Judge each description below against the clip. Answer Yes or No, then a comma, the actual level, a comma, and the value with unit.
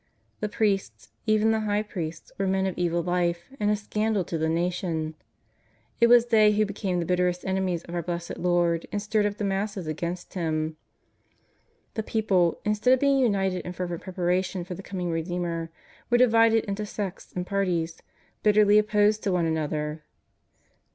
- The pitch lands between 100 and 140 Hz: No, high, 190 Hz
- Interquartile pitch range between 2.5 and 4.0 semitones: Yes, average, 3.5 semitones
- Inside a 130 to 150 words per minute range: No, average, 175 wpm